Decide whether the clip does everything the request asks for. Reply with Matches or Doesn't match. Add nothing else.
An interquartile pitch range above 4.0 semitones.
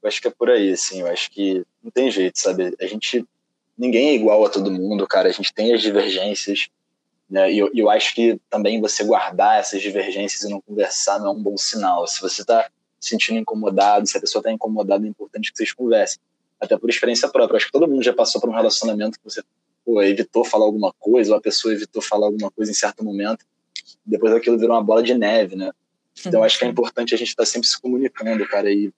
Doesn't match